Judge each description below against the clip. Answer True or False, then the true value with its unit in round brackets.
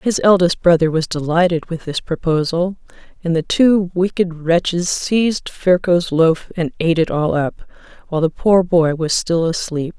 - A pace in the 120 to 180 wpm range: True (170 wpm)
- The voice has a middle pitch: True (170 Hz)